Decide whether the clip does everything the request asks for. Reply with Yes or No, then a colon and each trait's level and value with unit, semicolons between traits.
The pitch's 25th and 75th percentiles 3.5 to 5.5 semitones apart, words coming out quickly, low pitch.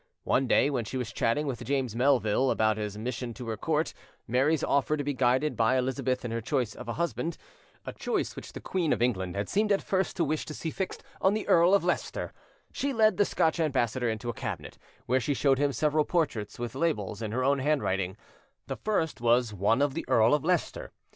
Yes: average, 5.0 semitones; fast, 215 wpm; low, 130 Hz